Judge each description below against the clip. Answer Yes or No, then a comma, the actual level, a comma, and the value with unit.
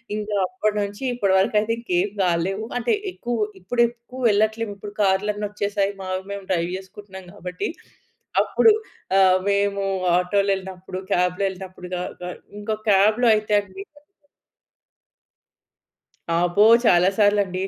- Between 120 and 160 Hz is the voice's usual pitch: No, high, 200 Hz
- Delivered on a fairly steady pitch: Yes, narrow, 2.1 semitones